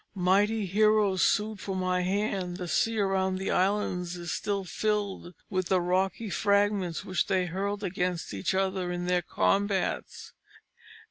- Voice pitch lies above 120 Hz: Yes, high, 190 Hz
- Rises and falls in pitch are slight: Yes, narrow, 2.1 semitones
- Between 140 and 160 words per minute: Yes, average, 145 wpm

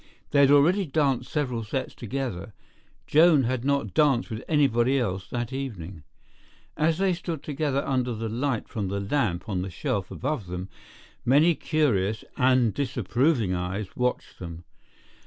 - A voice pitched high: No, low, 125 Hz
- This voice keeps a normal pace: Yes, average, 150 wpm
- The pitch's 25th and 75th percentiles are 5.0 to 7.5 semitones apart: Yes, wide, 5.6 semitones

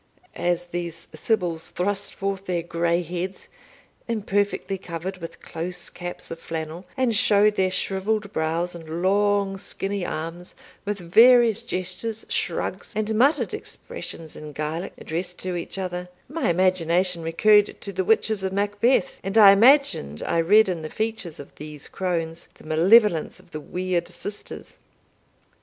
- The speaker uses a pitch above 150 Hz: Yes, medium, 185 Hz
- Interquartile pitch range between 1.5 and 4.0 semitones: Yes, average, 3.4 semitones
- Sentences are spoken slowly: No, average, 145 wpm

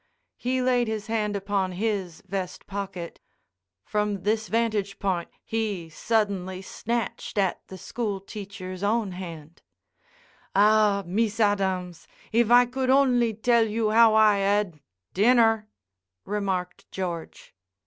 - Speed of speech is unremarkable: No, slow, 120 wpm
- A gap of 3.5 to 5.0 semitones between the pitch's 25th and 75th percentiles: No, average, 2.9 semitones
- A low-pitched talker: No, high, 205 Hz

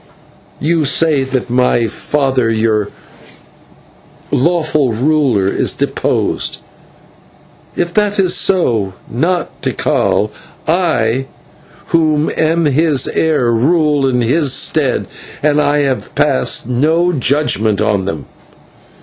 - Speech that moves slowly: Yes, slow, 105 wpm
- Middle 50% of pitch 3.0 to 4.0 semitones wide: No, average, 5.1 semitones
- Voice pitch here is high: No, medium, 140 Hz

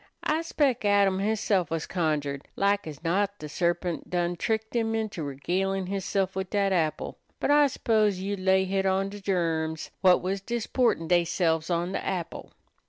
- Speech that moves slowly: No, average, 170 wpm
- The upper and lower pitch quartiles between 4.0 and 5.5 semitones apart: No, average, 3.0 semitones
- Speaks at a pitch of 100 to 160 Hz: No, high, 190 Hz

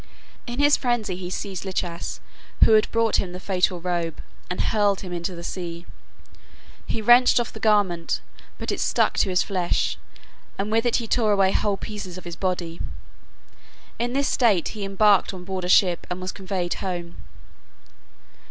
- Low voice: No, high, 190 Hz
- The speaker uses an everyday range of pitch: Yes, average, 3.3 semitones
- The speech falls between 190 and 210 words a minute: No, average, 175 wpm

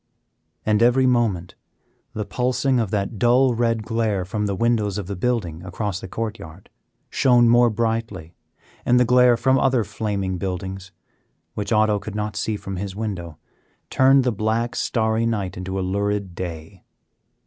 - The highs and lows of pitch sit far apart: No, average, 3.7 semitones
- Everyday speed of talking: Yes, average, 160 wpm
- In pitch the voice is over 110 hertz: No, low, 105 Hz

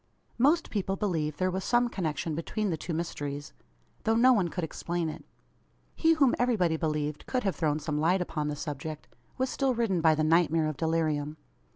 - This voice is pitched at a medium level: Yes, medium, 165 Hz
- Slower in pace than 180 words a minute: No, average, 195 wpm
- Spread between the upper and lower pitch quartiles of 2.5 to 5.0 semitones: No, wide, 5.4 semitones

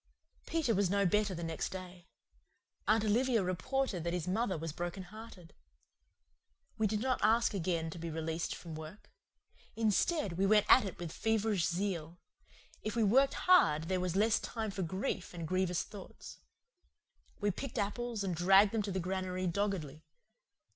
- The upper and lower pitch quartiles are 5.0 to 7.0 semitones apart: No, average, 3.8 semitones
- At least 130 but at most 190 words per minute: Yes, average, 165 wpm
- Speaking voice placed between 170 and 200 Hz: Yes, high, 190 Hz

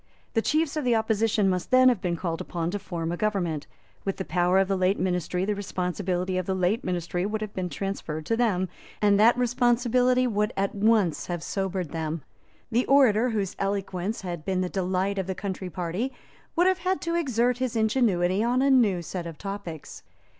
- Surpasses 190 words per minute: Yes, average, 200 wpm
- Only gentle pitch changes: No, average, 4.3 semitones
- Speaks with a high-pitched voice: Yes, high, 195 Hz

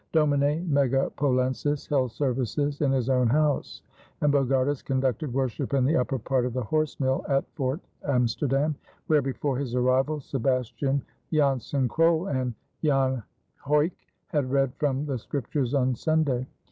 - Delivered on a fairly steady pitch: Yes, narrow, 2.2 semitones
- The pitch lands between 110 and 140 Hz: Yes, low, 135 Hz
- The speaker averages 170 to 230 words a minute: No, average, 145 wpm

